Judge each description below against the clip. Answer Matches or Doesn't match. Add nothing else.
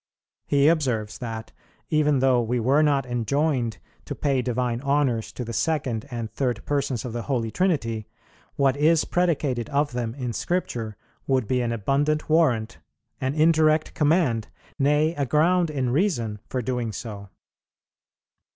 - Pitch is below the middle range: Matches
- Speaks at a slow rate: Doesn't match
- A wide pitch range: Doesn't match